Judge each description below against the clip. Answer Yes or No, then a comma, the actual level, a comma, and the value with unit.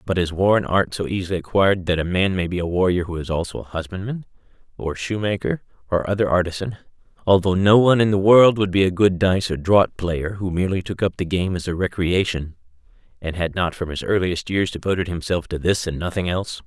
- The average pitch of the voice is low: Yes, very low, 90 Hz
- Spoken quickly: Yes, fast, 225 wpm